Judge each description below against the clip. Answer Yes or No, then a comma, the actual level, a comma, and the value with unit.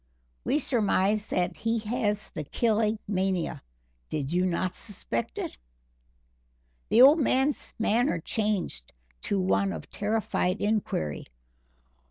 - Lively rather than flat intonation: No, average, 3.6 semitones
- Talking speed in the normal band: No, slow, 115 wpm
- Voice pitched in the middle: No, high, 205 Hz